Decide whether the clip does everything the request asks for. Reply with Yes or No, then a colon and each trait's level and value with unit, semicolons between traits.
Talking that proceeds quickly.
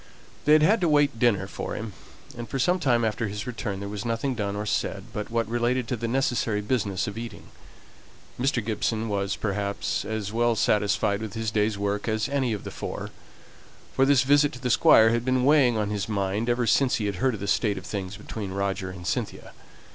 Yes: fast, 215 wpm